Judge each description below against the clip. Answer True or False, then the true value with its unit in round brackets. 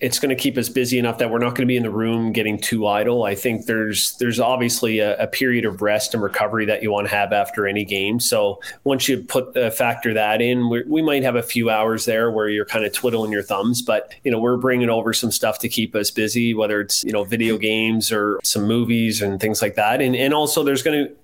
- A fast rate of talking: True (265 wpm)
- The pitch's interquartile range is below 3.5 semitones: True (2.5 semitones)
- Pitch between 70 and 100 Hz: False (115 Hz)